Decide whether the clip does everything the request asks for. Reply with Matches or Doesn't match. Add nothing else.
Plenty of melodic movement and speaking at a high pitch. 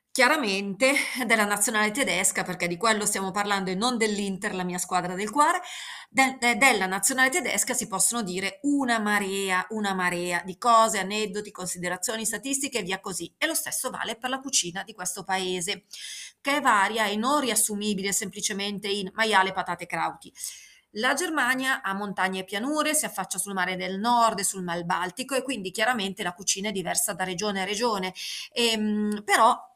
Doesn't match